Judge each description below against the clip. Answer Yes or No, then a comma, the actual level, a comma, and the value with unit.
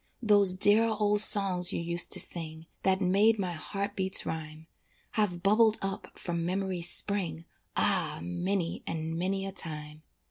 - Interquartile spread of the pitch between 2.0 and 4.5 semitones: Yes, average, 3.3 semitones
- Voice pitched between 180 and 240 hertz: Yes, medium, 185 Hz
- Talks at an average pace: Yes, average, 150 wpm